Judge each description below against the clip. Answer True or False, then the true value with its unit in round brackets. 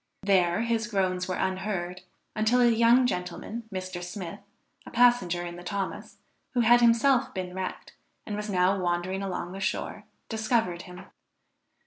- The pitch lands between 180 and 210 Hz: True (190 Hz)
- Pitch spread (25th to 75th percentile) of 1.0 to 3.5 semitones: False (4.1 semitones)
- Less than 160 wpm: True (150 wpm)